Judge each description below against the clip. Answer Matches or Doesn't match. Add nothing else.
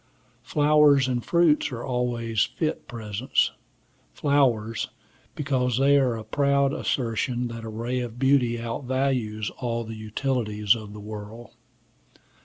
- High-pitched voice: Doesn't match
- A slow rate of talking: Matches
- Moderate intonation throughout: Matches